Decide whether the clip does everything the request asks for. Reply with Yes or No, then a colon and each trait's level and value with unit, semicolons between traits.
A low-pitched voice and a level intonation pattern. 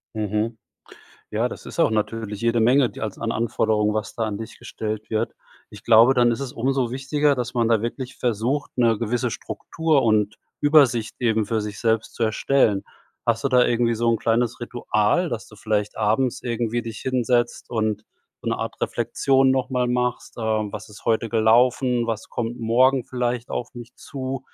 Yes: low, 115 Hz; narrow, 2.2 semitones